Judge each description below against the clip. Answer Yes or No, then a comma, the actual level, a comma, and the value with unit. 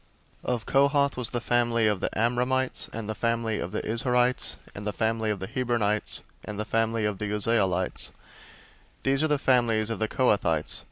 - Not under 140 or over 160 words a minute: No, average, 185 wpm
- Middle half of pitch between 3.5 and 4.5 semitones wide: No, average, 2.7 semitones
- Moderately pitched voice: No, low, 115 Hz